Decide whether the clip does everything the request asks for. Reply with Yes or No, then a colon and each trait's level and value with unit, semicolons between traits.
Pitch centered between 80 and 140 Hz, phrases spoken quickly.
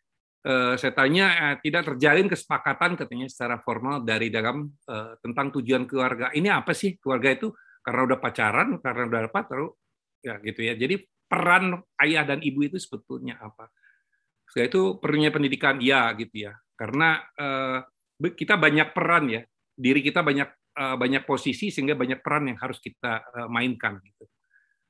Yes: low, 135 Hz; fast, 160 wpm